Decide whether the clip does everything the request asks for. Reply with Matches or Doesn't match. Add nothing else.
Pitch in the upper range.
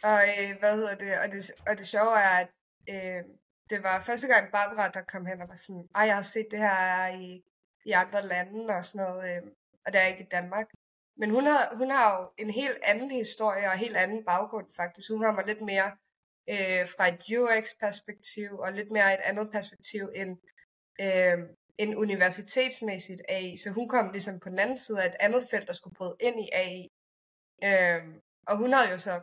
Matches